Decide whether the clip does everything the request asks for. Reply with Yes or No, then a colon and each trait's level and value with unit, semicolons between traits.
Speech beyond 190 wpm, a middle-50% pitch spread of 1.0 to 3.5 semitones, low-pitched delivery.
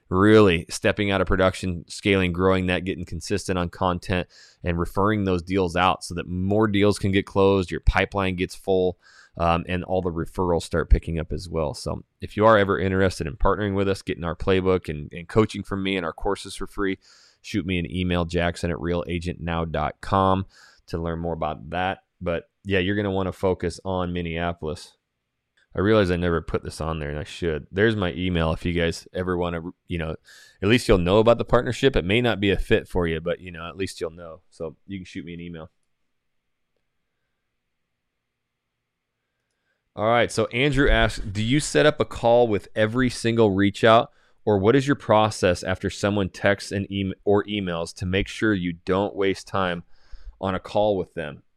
Yes: average, 200 wpm; average, 2.7 semitones; very low, 95 Hz